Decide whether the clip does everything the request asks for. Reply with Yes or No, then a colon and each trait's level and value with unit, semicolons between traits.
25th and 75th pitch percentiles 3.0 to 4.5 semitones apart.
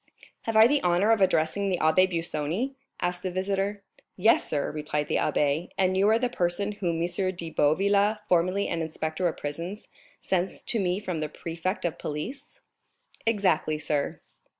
Yes: average, 3.8 semitones